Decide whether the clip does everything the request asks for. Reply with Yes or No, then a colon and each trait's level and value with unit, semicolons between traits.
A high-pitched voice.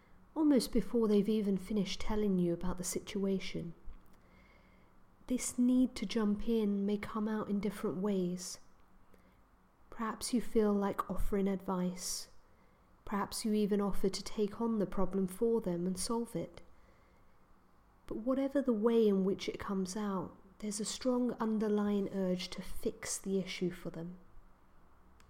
Yes: high, 200 Hz